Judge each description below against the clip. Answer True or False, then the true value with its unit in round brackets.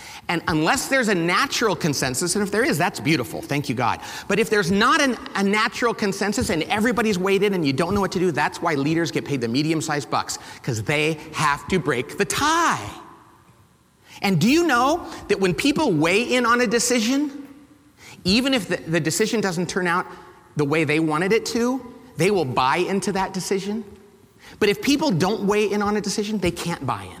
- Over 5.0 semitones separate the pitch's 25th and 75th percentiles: True (5.5 semitones)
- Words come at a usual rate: False (210 wpm)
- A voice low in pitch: False (200 Hz)